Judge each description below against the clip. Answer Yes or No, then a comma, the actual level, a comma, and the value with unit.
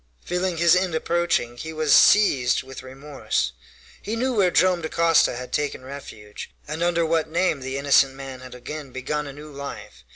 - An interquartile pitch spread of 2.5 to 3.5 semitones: No, average, 4.3 semitones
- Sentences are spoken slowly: No, average, 175 wpm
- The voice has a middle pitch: Yes, medium, 150 Hz